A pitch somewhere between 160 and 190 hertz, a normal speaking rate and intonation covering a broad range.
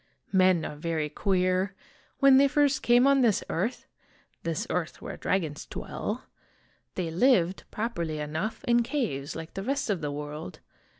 Yes: medium, 185 Hz; average, 155 wpm; wide, 7.0 semitones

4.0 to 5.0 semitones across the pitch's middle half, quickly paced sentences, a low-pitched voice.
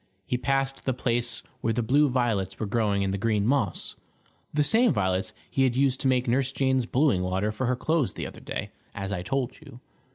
Yes: average, 4.5 semitones; fast, 215 wpm; low, 125 Hz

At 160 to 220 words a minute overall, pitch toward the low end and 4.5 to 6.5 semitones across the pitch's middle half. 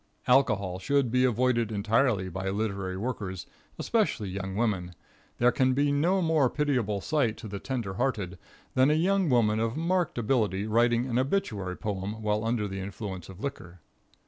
Yes: average, 165 wpm; low, 115 Hz; average, 5.1 semitones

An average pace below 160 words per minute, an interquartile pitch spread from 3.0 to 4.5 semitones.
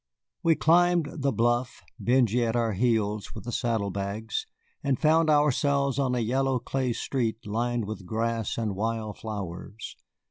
Yes: average, 150 wpm; average, 3.6 semitones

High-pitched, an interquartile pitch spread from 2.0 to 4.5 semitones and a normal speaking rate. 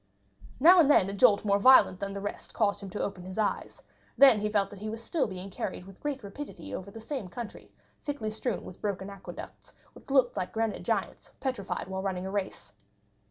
No: high, 205 Hz; average, 3.9 semitones; fast, 210 wpm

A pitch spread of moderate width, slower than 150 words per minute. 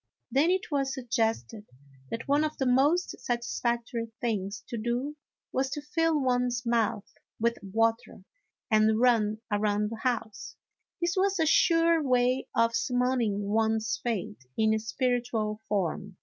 Yes: average, 3.4 semitones; average, 140 wpm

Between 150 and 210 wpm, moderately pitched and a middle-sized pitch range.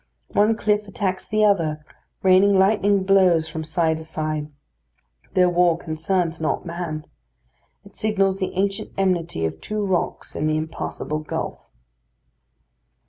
No: slow, 135 wpm; medium, 180 Hz; average, 3.7 semitones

